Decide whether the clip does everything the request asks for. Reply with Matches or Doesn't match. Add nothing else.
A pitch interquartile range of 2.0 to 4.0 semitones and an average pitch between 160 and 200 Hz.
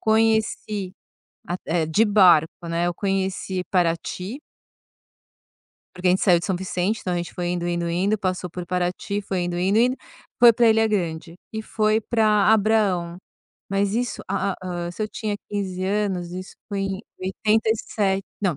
Matches